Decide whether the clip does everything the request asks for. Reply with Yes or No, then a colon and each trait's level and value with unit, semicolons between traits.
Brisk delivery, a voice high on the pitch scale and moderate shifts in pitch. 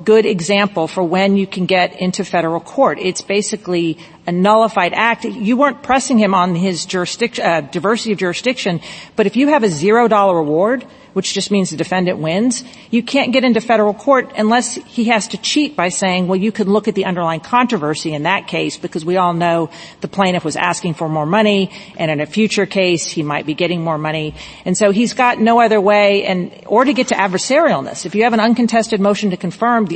Yes: fast, 210 wpm; high, 200 Hz; average, 4.3 semitones